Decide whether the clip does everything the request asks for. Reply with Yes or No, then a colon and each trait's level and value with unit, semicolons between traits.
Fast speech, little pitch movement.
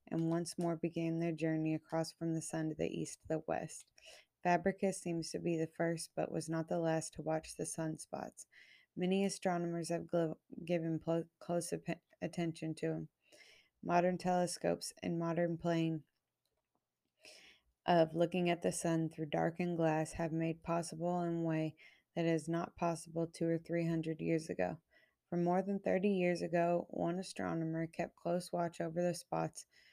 No: average, 170 wpm; narrow, 1.2 semitones